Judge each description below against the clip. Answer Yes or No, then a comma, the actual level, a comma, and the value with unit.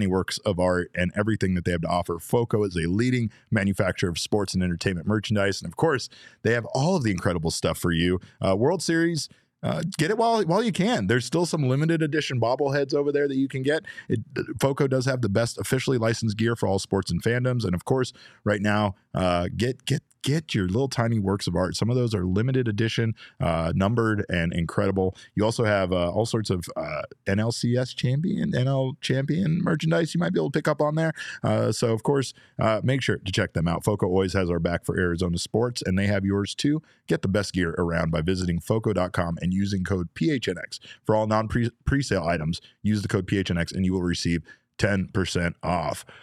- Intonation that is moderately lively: No, wide, 5.9 semitones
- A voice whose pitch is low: Yes, low, 110 Hz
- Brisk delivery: Yes, fast, 215 wpm